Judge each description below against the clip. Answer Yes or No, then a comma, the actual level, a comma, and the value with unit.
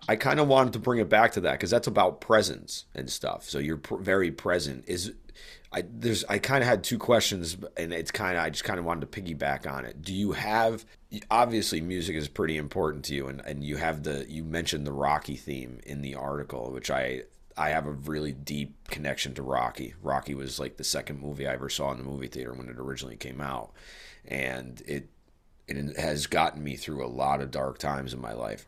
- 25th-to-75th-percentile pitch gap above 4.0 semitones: No, average, 3.4 semitones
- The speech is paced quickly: Yes, fast, 230 wpm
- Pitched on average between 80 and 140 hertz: No, very low, 70 Hz